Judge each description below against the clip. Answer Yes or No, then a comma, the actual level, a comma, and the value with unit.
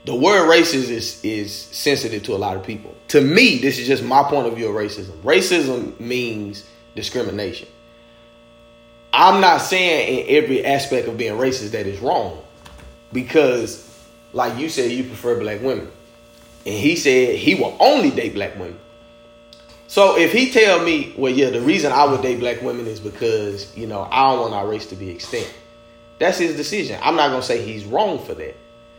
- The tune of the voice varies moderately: Yes, average, 3.2 semitones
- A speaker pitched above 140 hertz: No, low, 115 Hz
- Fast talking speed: No, average, 190 wpm